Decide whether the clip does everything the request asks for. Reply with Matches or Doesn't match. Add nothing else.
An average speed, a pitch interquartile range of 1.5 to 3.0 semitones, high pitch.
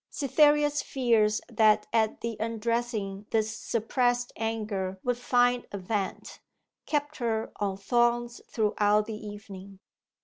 Doesn't match